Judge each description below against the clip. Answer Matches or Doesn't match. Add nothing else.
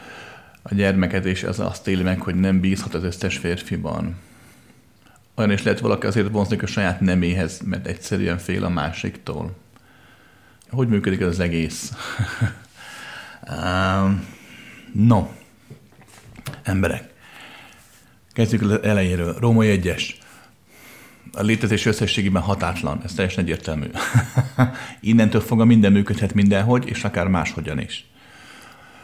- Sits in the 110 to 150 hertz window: Doesn't match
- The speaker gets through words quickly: Doesn't match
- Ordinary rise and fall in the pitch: Matches